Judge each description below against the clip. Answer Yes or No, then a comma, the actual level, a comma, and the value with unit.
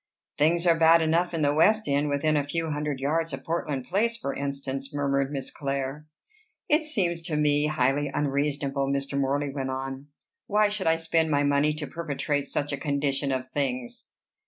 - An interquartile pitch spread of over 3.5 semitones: No, average, 2.8 semitones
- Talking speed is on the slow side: No, average, 180 wpm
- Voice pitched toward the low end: No, medium, 145 Hz